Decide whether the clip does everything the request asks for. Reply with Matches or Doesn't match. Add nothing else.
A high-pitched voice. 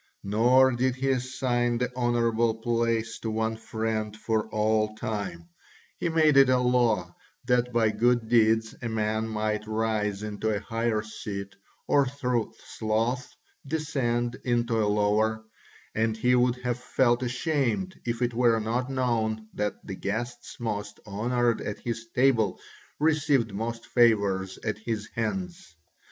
Doesn't match